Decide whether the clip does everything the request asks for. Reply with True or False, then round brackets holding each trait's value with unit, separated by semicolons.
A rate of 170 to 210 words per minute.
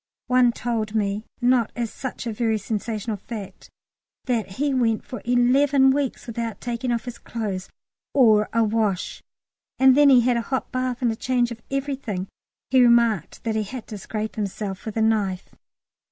True (175 wpm)